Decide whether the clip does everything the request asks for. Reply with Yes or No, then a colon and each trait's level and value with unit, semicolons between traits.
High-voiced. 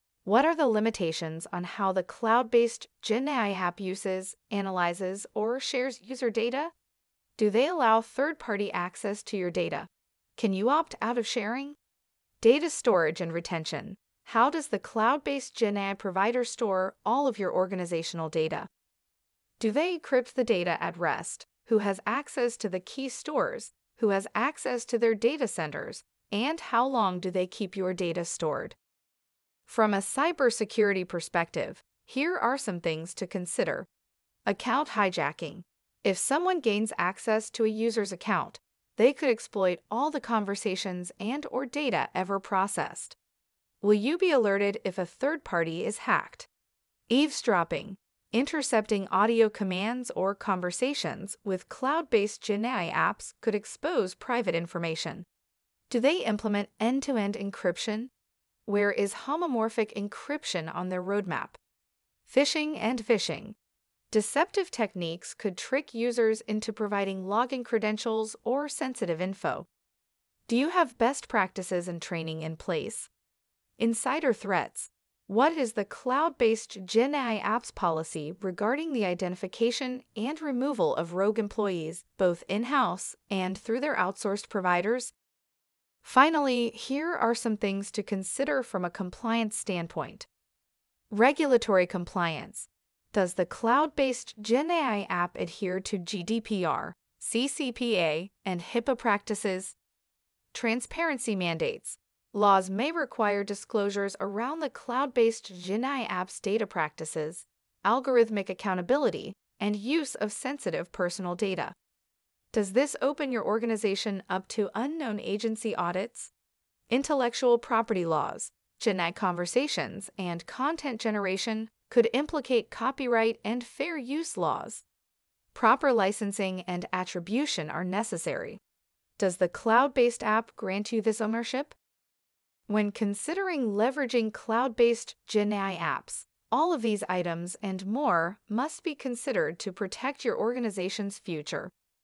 Yes: high, 215 Hz